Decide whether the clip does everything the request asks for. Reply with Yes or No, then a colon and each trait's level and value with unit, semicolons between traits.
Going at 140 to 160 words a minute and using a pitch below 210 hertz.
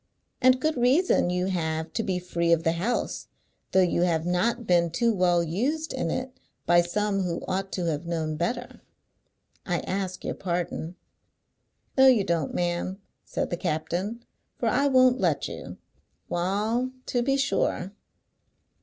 Yes: average, 155 wpm; medium, 185 Hz